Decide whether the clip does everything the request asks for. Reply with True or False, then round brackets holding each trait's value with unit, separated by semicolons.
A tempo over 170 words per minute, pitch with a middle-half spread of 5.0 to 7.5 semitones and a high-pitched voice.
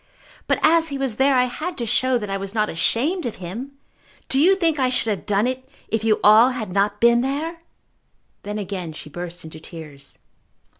True (205 wpm; 5.4 semitones; 230 Hz)